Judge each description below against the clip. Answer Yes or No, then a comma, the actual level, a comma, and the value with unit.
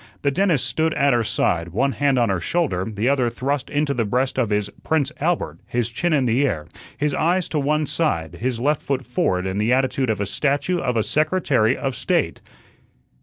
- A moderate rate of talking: No, fast, 210 wpm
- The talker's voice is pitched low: Yes, low, 130 Hz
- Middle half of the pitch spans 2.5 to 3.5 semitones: No, average, 4.9 semitones